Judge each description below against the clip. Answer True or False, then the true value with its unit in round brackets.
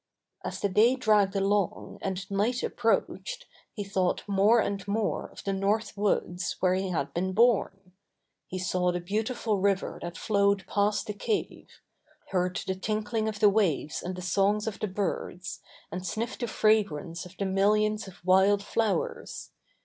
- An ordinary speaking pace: True (165 wpm)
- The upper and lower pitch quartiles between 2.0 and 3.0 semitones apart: True (2.4 semitones)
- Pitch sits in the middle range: False (200 Hz)